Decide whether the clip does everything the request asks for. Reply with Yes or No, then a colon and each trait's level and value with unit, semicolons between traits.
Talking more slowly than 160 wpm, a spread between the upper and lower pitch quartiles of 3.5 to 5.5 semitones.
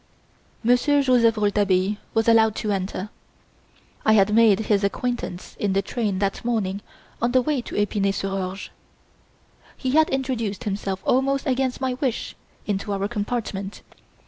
Yes: average, 145 wpm; average, 3.9 semitones